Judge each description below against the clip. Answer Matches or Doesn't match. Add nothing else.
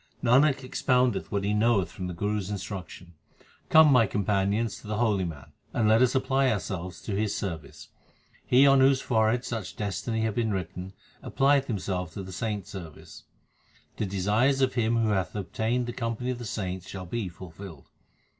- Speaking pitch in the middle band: Doesn't match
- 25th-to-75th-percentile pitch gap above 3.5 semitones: Matches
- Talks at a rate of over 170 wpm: Matches